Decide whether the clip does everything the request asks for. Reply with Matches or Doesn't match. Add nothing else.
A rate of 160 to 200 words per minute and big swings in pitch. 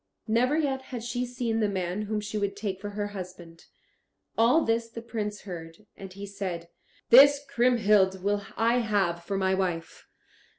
Doesn't match